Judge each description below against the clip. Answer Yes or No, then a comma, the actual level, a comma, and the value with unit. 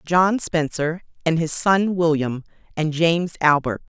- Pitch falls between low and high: Yes, medium, 160 Hz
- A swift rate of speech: No, slow, 135 wpm